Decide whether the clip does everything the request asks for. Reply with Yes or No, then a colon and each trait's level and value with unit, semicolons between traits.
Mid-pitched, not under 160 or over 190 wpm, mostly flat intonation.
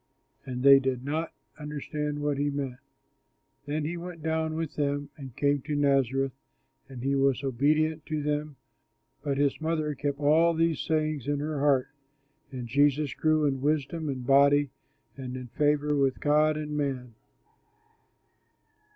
No: medium, 145 Hz; average, 150 wpm; narrow, 2.0 semitones